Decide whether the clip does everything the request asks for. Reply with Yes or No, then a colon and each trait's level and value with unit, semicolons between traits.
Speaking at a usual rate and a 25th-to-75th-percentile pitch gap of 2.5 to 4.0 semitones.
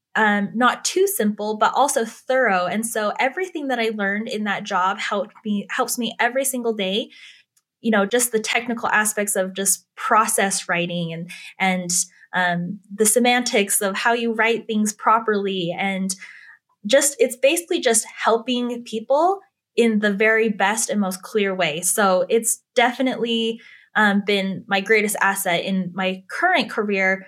Yes: average, 155 wpm; average, 3.6 semitones